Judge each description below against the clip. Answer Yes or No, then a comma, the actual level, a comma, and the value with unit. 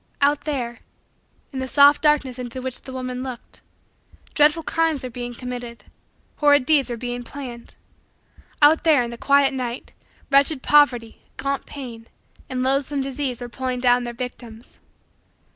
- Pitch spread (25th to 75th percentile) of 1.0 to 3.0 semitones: Yes, average, 2.7 semitones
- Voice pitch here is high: Yes, very high, 260 Hz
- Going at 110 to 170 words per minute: Yes, average, 150 wpm